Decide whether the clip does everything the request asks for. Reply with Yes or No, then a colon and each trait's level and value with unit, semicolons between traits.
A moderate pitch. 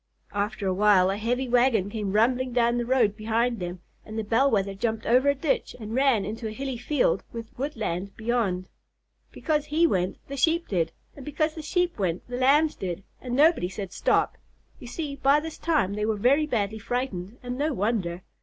No: high, 235 Hz